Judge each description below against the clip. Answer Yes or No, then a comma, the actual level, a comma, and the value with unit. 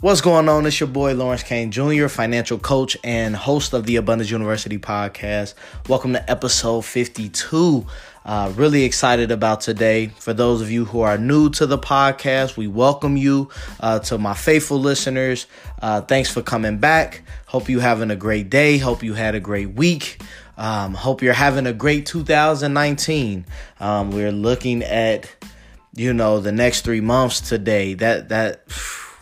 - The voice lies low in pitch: Yes, low, 120 Hz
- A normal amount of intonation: Yes, average, 4.1 semitones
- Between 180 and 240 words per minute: No, average, 170 wpm